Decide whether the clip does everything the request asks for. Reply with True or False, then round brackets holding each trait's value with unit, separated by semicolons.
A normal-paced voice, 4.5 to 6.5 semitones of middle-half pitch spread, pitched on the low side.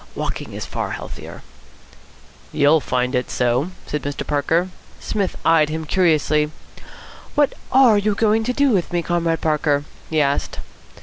False (145 wpm; 5.2 semitones; 160 Hz)